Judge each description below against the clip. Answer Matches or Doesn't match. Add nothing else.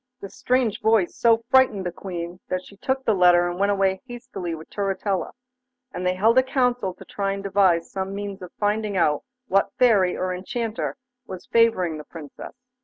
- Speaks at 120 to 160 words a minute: Doesn't match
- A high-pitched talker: Matches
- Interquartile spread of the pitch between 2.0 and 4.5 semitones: Matches